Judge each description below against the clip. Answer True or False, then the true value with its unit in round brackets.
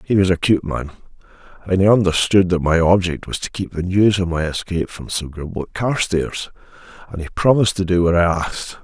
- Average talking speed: False (210 wpm)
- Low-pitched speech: True (90 Hz)